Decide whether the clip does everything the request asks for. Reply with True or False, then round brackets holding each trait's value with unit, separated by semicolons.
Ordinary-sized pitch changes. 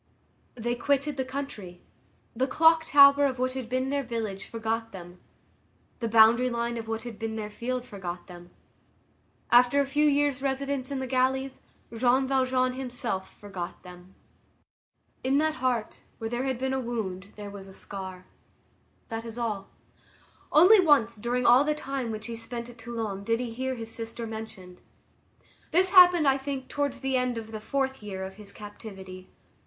True (3.6 semitones)